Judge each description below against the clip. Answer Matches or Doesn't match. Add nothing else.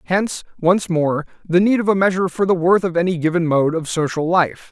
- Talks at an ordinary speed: Doesn't match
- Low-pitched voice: Doesn't match